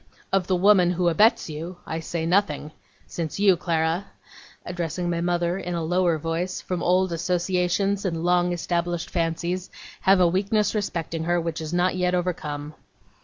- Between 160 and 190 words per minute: Yes, average, 165 wpm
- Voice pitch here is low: No, medium, 175 Hz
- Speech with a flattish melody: Yes, narrow, 1.8 semitones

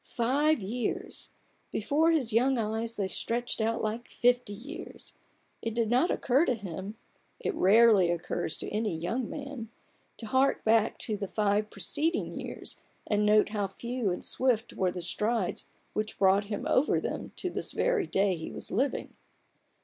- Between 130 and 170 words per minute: Yes, average, 165 wpm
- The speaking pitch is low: No, high, 225 Hz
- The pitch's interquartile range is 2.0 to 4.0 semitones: Yes, average, 3.6 semitones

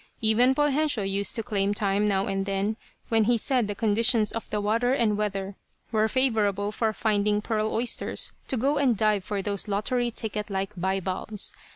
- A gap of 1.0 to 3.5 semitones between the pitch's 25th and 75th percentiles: Yes, narrow, 2.5 semitones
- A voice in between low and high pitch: No, high, 215 Hz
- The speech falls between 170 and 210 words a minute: Yes, average, 180 wpm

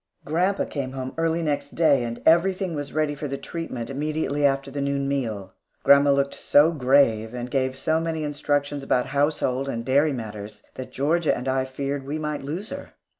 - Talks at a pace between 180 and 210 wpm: Yes, average, 190 wpm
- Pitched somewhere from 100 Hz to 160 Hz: Yes, medium, 140 Hz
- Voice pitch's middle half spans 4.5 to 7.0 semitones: No, average, 2.8 semitones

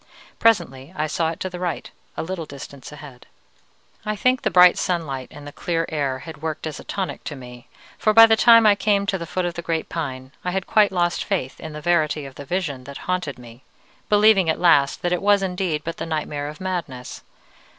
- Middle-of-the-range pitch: Yes, medium, 165 Hz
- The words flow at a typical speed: No, fast, 225 wpm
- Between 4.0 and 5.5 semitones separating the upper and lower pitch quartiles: Yes, average, 4.5 semitones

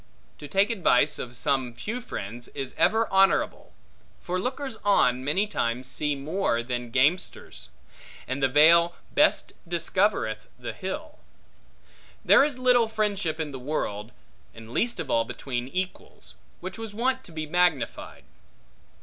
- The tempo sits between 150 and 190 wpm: No, average, 140 wpm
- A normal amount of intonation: No, wide, 8.5 semitones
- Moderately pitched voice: Yes, medium, 160 Hz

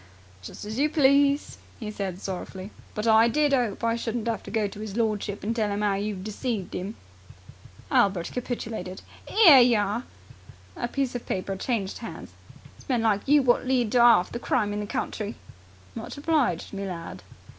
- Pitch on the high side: Yes, high, 220 Hz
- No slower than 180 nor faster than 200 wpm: Yes, average, 185 wpm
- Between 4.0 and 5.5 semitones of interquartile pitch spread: No, average, 3.4 semitones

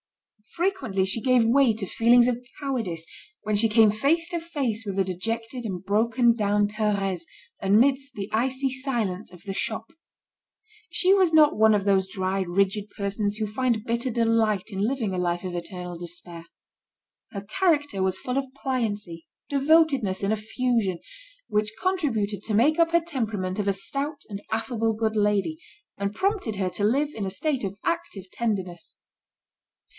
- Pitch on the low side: No, high, 220 Hz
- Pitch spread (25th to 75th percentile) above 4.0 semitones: Yes, average, 4.8 semitones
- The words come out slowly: No, average, 165 wpm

